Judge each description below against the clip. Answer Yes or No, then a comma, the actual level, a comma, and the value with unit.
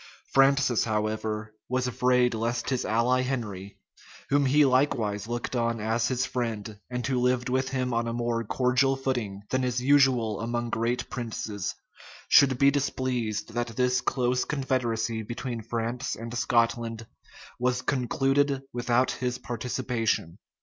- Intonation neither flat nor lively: No, narrow, 2.0 semitones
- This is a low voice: Yes, low, 120 Hz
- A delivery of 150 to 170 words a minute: No, average, 140 wpm